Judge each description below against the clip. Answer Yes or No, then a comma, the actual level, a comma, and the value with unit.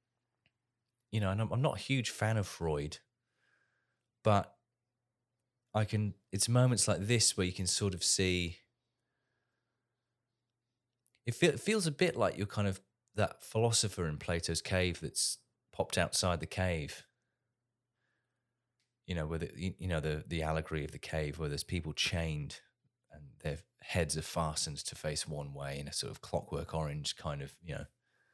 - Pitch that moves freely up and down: Yes, wide, 6.9 semitones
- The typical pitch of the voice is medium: No, low, 100 Hz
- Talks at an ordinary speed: Yes, average, 165 wpm